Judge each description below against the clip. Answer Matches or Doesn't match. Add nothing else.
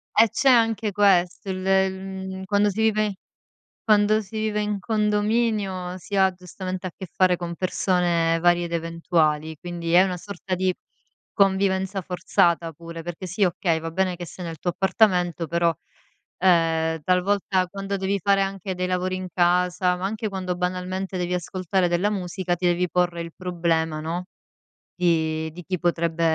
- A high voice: Doesn't match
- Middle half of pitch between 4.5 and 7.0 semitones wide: Doesn't match